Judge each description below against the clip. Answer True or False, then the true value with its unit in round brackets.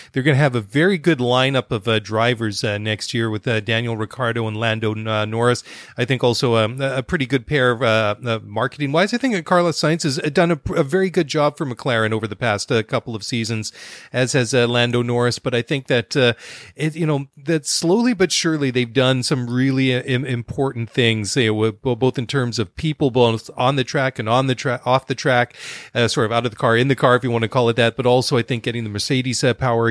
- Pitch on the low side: True (125 Hz)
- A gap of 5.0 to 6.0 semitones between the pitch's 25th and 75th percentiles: False (3.1 semitones)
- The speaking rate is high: True (245 wpm)